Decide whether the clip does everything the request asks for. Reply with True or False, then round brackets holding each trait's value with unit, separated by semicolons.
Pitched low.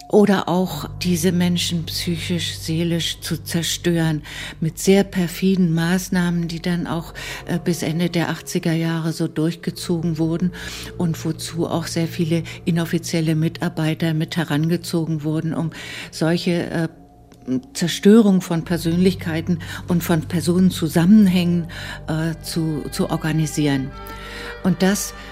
False (165 Hz)